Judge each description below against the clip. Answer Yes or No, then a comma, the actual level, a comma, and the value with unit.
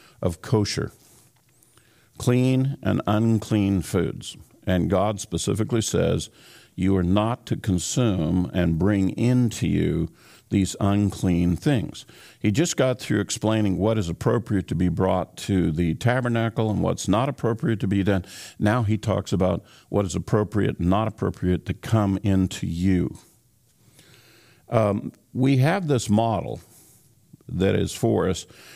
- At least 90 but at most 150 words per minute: Yes, average, 140 wpm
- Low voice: Yes, low, 105 Hz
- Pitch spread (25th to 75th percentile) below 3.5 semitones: No, average, 3.9 semitones